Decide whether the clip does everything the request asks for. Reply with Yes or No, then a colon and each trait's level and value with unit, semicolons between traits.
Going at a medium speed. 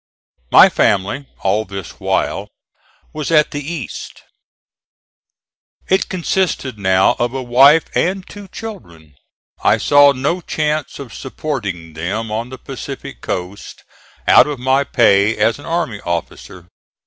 No: slow, 130 wpm